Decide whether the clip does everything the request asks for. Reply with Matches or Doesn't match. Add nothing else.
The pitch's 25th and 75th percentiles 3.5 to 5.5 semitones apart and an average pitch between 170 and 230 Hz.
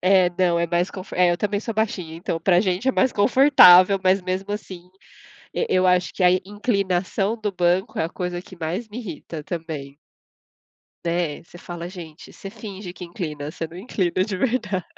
Doesn't match